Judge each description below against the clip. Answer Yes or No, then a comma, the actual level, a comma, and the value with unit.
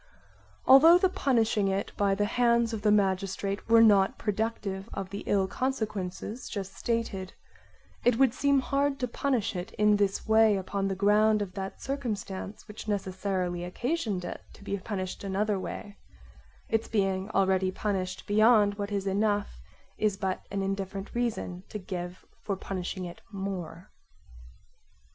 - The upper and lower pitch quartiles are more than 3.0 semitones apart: No, narrow, 2.6 semitones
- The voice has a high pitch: Yes, high, 205 Hz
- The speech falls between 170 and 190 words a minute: No, average, 150 wpm